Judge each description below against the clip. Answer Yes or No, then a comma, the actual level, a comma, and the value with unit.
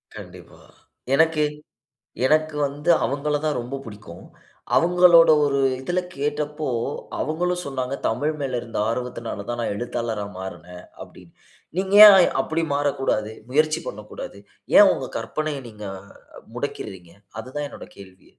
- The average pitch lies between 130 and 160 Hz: Yes, medium, 140 Hz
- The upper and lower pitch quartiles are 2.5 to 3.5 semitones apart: No, average, 5.3 semitones